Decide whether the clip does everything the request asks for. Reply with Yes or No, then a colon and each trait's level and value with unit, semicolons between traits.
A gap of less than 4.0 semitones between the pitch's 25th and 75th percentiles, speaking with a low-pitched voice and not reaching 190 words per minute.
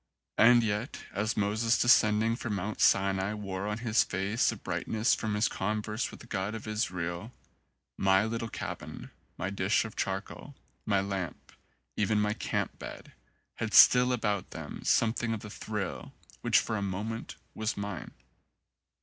Yes: narrow, 2.4 semitones; low, 105 Hz; average, 155 wpm